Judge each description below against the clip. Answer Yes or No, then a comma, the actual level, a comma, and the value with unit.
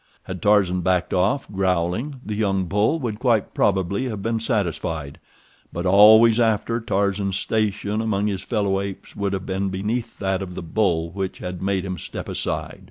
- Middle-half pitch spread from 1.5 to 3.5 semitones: Yes, average, 2.7 semitones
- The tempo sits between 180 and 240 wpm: No, average, 170 wpm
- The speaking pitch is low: Yes, low, 100 Hz